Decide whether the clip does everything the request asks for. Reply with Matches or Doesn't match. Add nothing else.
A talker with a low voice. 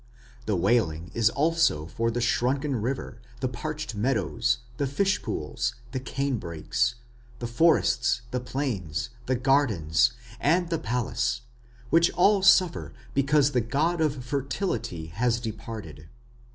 Matches